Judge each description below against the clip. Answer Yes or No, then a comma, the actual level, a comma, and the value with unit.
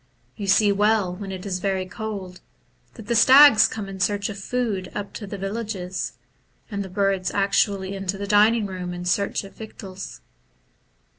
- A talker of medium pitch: No, high, 200 Hz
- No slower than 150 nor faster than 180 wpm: Yes, average, 175 wpm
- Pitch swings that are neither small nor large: No, narrow, 1.9 semitones